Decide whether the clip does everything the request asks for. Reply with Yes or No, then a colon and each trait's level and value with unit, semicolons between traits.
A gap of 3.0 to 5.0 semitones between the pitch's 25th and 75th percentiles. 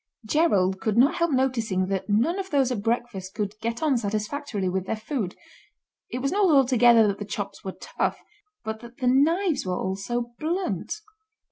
No: wide, 5.5 semitones